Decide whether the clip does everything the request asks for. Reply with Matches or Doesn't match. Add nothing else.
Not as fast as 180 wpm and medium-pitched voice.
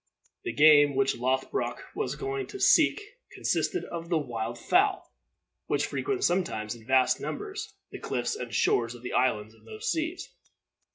Matches